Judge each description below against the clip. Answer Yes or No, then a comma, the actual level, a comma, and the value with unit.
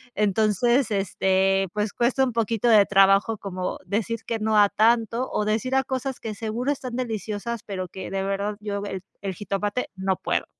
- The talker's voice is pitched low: No, high, 210 Hz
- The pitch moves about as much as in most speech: Yes, average, 3.0 semitones